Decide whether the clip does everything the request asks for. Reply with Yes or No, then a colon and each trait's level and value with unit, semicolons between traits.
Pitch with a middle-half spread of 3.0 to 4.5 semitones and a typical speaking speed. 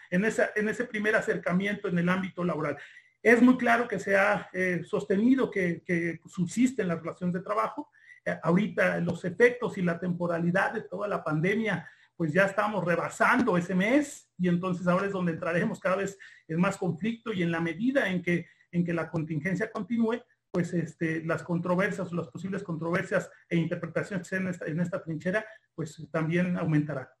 Yes: average, 3.8 semitones; average, 180 wpm